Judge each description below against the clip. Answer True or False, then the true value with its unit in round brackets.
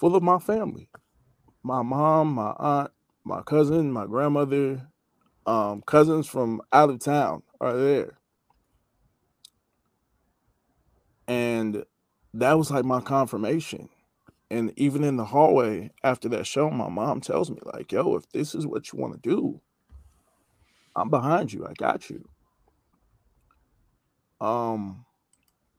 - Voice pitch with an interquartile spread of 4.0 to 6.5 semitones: True (5.0 semitones)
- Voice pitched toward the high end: False (135 Hz)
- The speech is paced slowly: True (125 wpm)